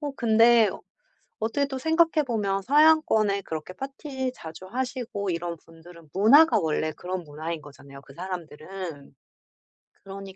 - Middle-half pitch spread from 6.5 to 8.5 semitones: Yes, wide, 7.6 semitones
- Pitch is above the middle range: Yes, high, 195 Hz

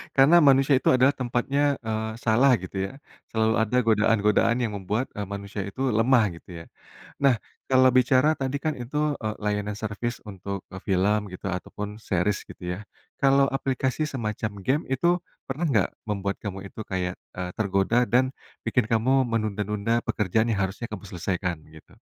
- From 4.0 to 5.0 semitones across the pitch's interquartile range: Yes, average, 4.4 semitones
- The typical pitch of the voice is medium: No, low, 110 Hz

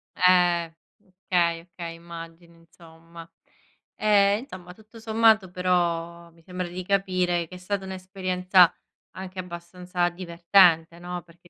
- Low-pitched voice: No, medium, 180 Hz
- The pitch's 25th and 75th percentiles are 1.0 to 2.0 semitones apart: Yes, narrow, 1.6 semitones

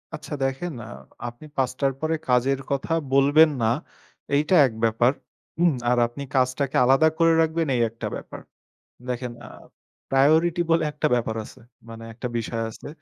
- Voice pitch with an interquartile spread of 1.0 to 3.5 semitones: No, average, 4.3 semitones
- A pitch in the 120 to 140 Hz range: Yes, low, 135 Hz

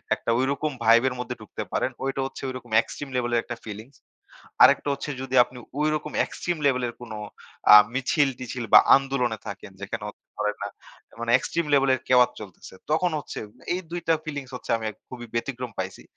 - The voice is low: Yes, low, 125 Hz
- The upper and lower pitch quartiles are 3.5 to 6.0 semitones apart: No, average, 2.9 semitones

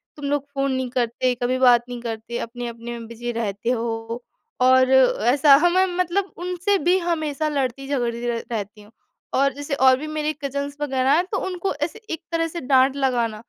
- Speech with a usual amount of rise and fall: Yes, average, 4.1 semitones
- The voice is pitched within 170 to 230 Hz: No, very high, 265 Hz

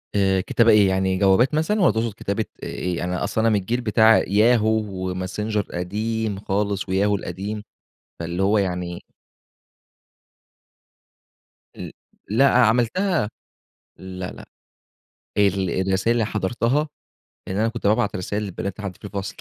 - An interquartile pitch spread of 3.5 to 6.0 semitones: No, average, 2.9 semitones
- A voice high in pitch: No, low, 105 Hz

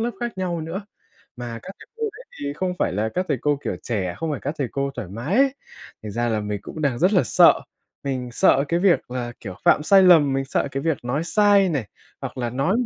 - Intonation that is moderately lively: No, wide, 7.0 semitones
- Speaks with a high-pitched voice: No, medium, 140 Hz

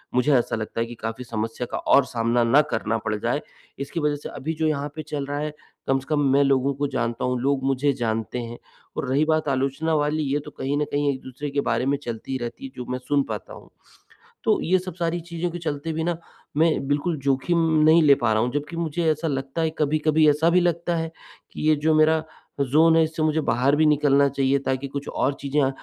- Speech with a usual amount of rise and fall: Yes, average, 3.0 semitones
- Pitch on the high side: No, medium, 145 Hz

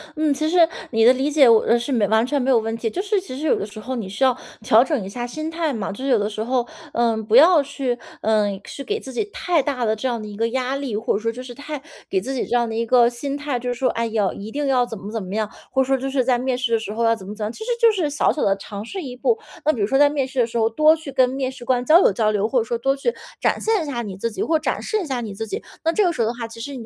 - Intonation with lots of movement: No, average, 4.1 semitones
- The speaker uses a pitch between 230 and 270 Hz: Yes, very high, 250 Hz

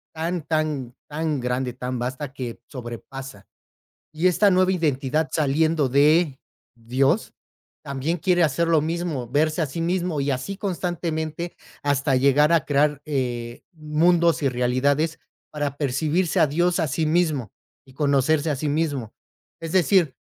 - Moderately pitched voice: Yes, medium, 150 Hz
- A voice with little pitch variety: No, average, 3.6 semitones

